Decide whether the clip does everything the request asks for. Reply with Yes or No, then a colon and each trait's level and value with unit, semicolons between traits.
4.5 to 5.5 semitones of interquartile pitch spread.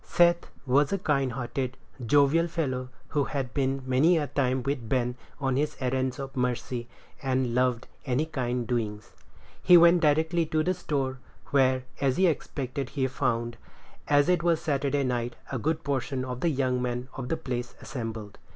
No: average, 2.9 semitones